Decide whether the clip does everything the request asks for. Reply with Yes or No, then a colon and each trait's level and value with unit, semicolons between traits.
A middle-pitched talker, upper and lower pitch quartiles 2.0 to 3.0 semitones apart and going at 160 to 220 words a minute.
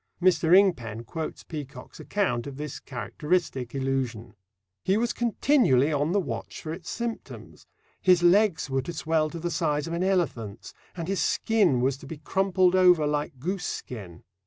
No: medium, 160 Hz; wide, 5.5 semitones; average, 165 wpm